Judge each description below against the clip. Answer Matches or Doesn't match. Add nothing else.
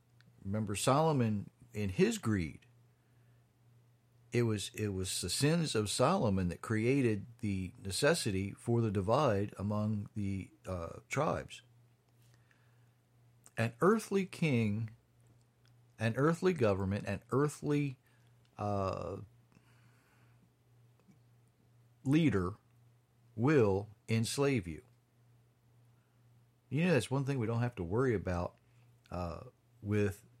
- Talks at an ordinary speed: Doesn't match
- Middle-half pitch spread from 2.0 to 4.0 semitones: Matches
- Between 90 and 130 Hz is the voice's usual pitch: Matches